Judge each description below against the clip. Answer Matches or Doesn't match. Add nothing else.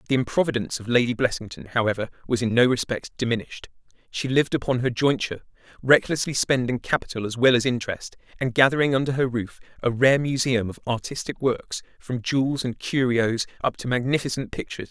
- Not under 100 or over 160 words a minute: Doesn't match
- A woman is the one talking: Doesn't match